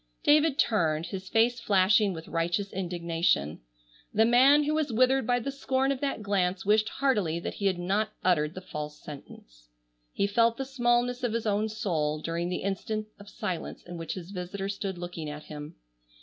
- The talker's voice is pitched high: Yes, high, 200 Hz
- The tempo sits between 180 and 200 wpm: Yes, average, 185 wpm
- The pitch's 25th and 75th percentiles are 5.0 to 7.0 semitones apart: Yes, wide, 5.5 semitones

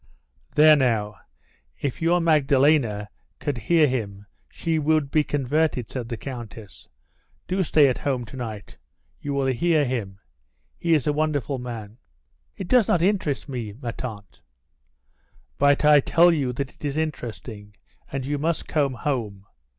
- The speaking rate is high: No, average, 150 wpm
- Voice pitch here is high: No, low, 135 Hz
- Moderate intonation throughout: Yes, average, 4.7 semitones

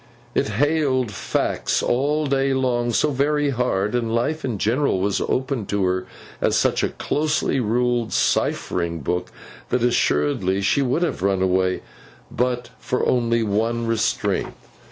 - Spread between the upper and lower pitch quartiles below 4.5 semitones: No, average, 5.0 semitones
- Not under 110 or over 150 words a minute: Yes, average, 145 wpm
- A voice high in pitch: No, low, 120 Hz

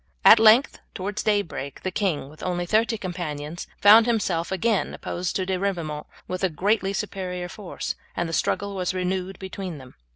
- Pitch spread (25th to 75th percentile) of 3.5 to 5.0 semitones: No, average, 2.7 semitones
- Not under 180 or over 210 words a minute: No, average, 170 wpm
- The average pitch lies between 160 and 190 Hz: Yes, medium, 185 Hz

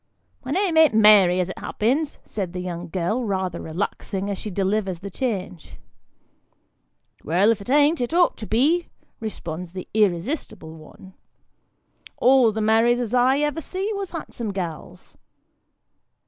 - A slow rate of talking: No, average, 155 wpm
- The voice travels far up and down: Yes, wide, 6.1 semitones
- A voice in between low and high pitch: No, high, 215 Hz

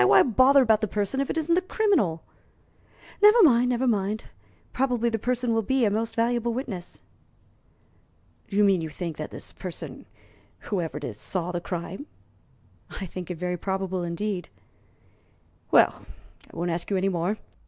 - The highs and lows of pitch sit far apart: Yes, wide, 5.7 semitones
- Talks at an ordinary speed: Yes, average, 165 wpm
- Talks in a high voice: Yes, high, 205 Hz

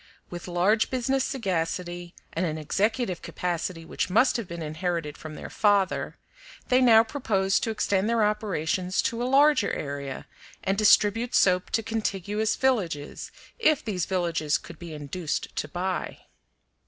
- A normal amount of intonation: Yes, average, 4.7 semitones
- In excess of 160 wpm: No, average, 145 wpm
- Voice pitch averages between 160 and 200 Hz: Yes, high, 190 Hz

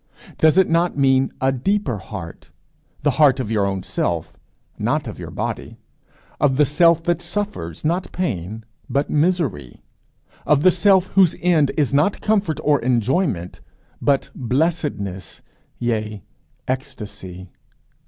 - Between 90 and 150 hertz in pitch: Yes, medium, 140 Hz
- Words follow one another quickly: No, slow, 135 wpm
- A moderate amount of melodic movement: No, wide, 7.8 semitones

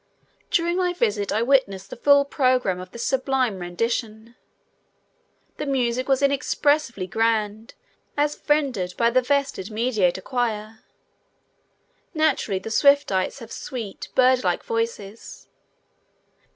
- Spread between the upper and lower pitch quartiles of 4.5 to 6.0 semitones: Yes, average, 4.8 semitones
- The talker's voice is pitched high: Yes, high, 235 Hz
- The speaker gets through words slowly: Yes, slow, 115 wpm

